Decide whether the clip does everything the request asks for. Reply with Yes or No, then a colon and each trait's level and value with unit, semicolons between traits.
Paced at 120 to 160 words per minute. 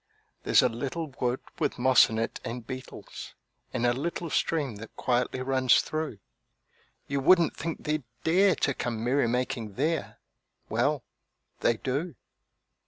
Yes: average, 140 wpm